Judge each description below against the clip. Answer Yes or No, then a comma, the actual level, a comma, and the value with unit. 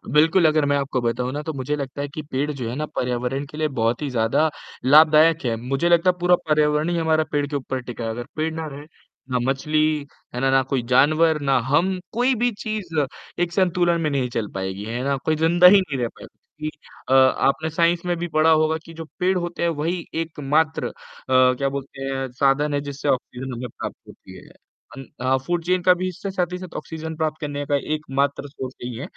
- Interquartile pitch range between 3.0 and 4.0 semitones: Yes, average, 3.6 semitones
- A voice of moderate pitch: Yes, medium, 150 Hz